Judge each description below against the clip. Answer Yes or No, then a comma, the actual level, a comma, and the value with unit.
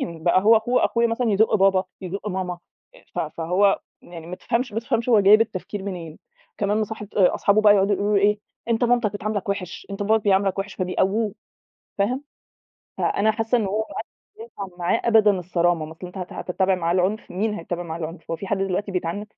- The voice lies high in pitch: Yes, high, 200 Hz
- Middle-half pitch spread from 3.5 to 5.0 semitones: No, average, 2.9 semitones